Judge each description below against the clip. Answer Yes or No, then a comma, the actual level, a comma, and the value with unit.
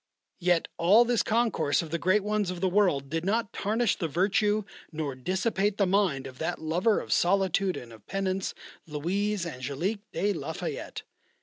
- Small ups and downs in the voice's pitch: No, average, 4.1 semitones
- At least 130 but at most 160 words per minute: No, average, 175 wpm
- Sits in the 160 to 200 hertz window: Yes, medium, 185 Hz